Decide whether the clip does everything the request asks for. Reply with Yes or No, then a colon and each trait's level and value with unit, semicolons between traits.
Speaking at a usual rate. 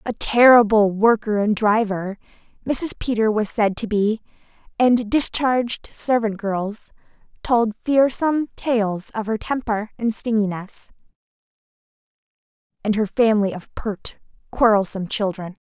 No: slow, 115 wpm